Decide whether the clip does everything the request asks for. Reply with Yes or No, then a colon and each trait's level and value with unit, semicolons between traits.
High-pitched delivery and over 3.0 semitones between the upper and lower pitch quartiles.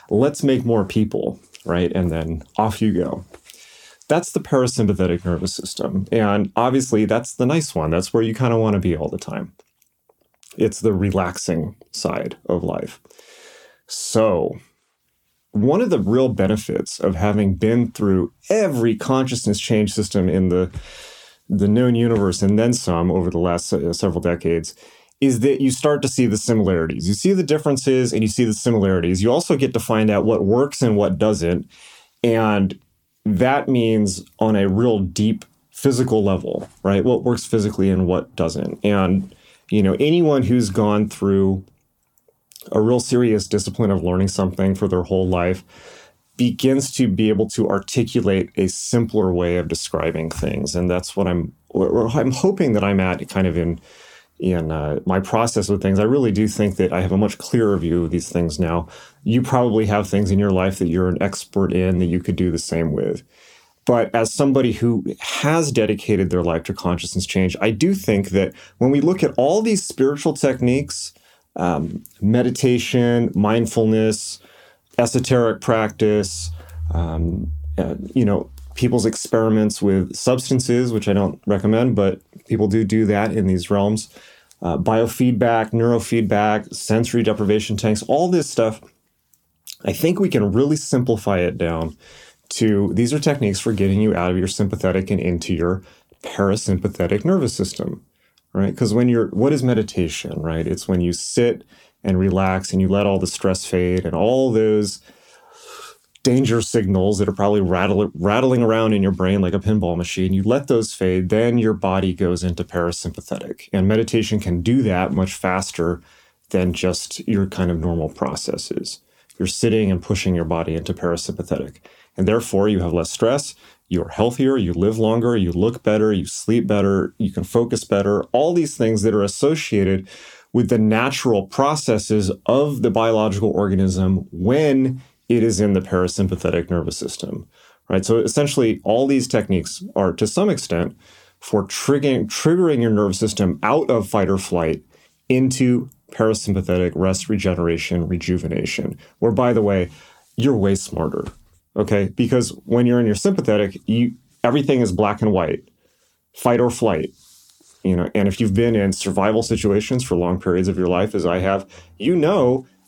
No: low, 105 Hz; average, 4.2 semitones